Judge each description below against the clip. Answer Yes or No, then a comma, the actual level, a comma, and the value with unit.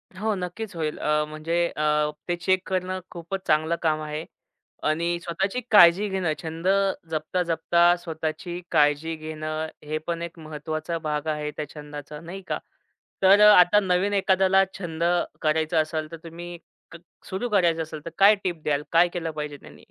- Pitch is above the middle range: No, medium, 165 Hz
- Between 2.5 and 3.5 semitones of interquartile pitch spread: Yes, average, 2.8 semitones